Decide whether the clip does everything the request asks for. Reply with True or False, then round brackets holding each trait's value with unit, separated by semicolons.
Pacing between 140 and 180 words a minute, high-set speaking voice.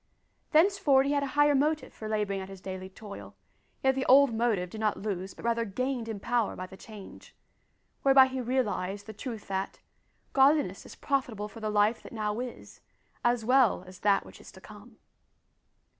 False (190 wpm; 225 Hz)